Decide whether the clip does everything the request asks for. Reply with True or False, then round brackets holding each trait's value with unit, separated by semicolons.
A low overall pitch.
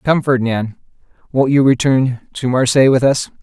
True (130 Hz)